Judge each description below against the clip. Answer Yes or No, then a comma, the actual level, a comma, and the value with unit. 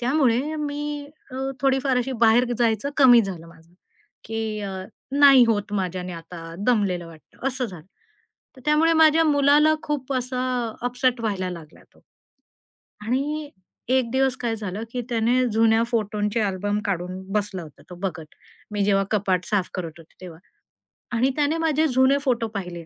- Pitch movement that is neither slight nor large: No, wide, 5.9 semitones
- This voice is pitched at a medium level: No, high, 230 Hz